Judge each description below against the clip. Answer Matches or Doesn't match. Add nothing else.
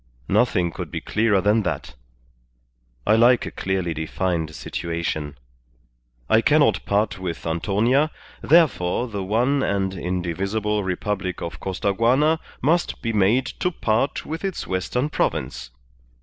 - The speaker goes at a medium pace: Doesn't match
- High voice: Doesn't match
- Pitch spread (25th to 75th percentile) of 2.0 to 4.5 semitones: Doesn't match